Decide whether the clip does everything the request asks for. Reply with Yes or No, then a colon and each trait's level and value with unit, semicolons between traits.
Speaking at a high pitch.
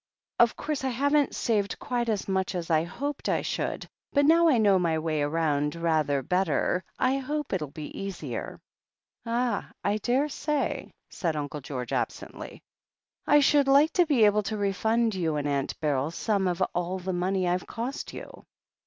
Yes: high, 195 Hz